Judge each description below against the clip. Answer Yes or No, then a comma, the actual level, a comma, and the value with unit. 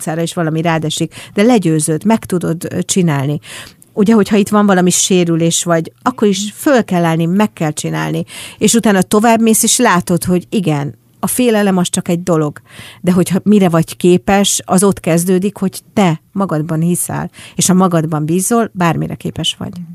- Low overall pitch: No, medium, 180 Hz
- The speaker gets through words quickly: Yes, fast, 165 wpm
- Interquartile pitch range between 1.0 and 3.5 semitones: No, average, 3.9 semitones